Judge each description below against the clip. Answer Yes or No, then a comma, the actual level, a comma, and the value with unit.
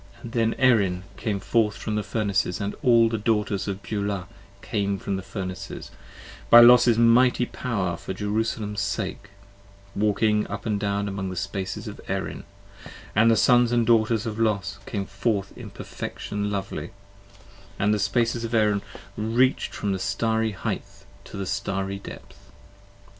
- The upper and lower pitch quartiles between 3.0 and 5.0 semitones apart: No, narrow, 2.5 semitones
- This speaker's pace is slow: No, average, 155 wpm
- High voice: No, low, 105 Hz